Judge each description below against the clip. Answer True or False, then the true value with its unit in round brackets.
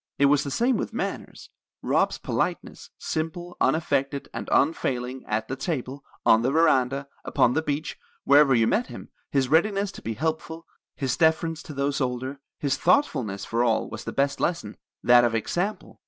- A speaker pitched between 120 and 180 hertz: True (140 Hz)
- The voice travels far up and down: False (4.3 semitones)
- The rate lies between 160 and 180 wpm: True (170 wpm)